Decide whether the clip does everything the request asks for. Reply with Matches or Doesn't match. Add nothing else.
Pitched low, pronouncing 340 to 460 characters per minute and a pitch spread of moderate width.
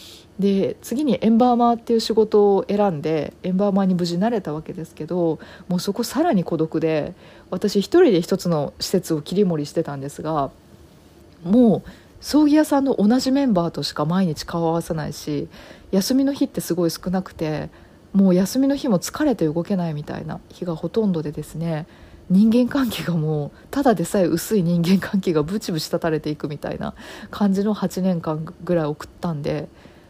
Doesn't match